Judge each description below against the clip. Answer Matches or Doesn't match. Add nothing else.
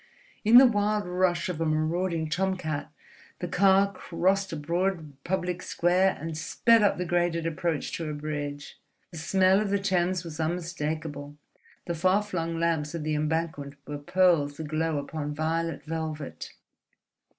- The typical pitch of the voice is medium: Matches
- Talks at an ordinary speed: Matches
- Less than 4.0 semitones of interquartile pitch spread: Matches